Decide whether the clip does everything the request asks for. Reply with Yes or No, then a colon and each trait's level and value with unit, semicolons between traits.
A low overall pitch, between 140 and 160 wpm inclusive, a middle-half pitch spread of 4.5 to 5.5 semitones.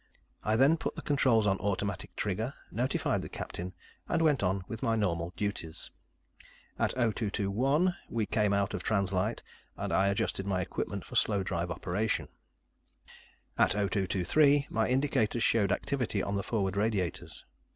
No: low, 105 Hz; average, 150 wpm; average, 3.2 semitones